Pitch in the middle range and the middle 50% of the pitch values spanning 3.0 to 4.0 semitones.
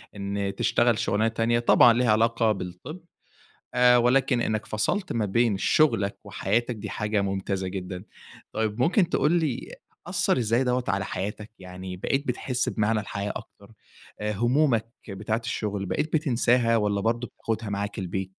No: low, 110 Hz; average, 3.5 semitones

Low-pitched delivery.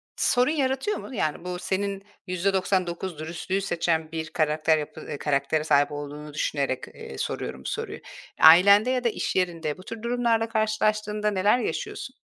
No: medium, 185 Hz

